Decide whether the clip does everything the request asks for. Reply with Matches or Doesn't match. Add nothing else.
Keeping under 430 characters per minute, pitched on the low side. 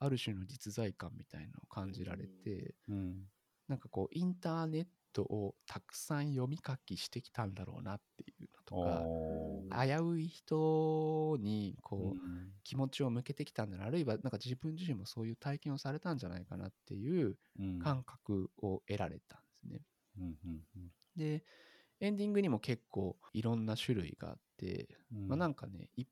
Matches